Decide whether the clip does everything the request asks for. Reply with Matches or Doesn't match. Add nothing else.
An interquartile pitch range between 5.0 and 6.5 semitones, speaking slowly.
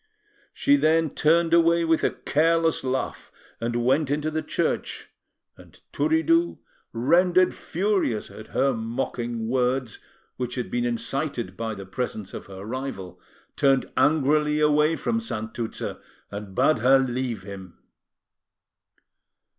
Matches